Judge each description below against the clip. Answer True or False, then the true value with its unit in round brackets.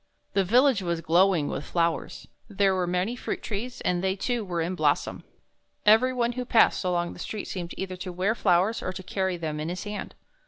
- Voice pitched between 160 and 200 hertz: True (190 Hz)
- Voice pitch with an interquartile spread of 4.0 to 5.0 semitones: False (3.5 semitones)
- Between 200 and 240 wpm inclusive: True (205 wpm)